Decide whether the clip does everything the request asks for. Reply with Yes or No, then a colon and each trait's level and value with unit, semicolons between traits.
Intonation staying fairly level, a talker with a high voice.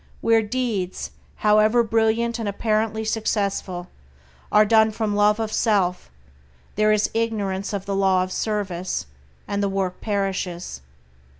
Yes: narrow, 2.2 semitones; high, 210 Hz